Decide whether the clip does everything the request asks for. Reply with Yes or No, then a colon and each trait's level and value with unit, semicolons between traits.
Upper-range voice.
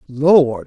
No: medium, 140 Hz